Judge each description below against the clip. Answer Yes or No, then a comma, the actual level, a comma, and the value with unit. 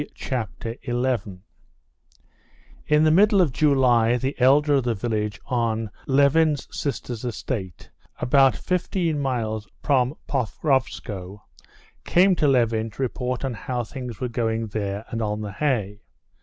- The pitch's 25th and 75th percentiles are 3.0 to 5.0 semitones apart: Yes, average, 4.0 semitones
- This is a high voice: No, low, 125 Hz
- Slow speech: Yes, slow, 130 wpm